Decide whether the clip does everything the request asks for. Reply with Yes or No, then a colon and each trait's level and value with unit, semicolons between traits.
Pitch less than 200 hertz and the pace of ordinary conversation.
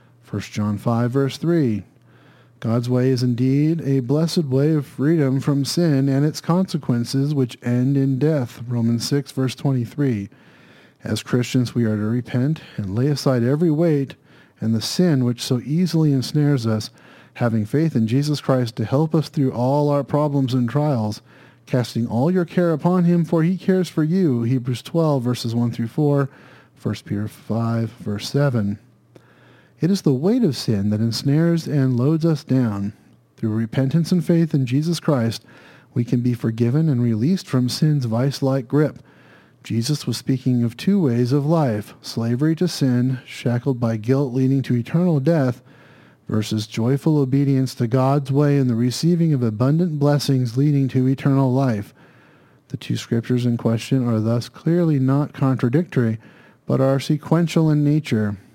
Yes: low, 135 Hz; average, 165 wpm